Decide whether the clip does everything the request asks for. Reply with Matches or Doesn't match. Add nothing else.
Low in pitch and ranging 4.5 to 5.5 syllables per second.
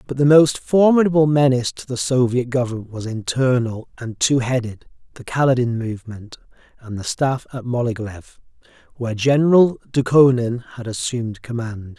Matches